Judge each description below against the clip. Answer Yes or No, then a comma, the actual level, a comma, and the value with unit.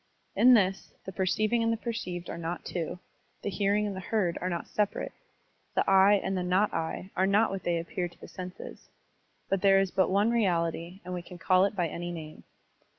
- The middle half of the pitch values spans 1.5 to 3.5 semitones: Yes, narrow, 2.4 semitones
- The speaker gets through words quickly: Yes, fast, 215 wpm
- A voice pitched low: No, high, 190 Hz